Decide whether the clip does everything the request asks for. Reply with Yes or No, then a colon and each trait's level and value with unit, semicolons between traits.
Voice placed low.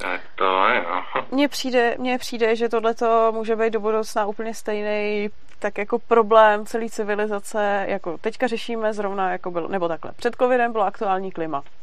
No: high, 220 Hz